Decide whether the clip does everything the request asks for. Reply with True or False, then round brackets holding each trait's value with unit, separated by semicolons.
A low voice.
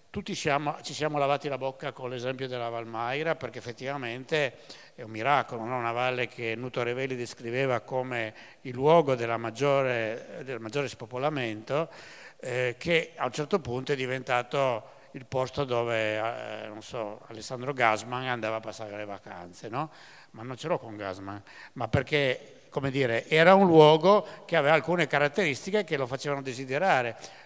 True (130 Hz)